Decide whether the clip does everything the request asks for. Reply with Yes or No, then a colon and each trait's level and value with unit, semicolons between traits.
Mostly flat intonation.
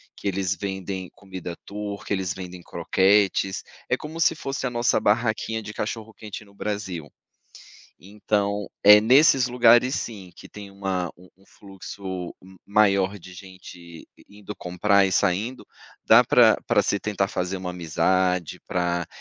Yes: narrow, 2.3 semitones